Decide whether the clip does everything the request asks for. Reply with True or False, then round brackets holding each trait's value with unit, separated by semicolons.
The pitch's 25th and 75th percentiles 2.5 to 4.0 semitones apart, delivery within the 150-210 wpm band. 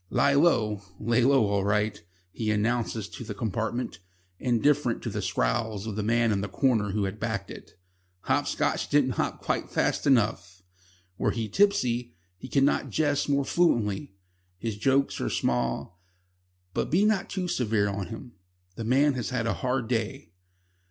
False (4.5 semitones; 165 wpm)